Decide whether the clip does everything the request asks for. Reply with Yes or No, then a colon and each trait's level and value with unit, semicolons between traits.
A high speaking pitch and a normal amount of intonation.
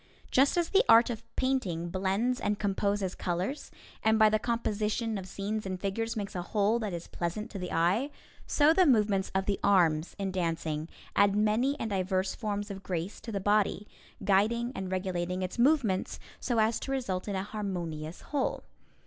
Yes: high, 200 Hz; average, 3.4 semitones